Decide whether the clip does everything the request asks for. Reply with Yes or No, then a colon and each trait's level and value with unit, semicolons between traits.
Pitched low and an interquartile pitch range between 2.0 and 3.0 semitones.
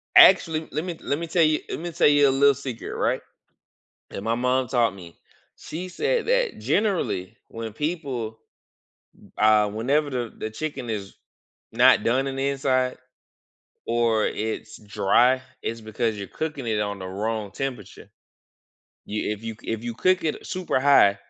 No: low, 125 Hz; average, 5.2 semitones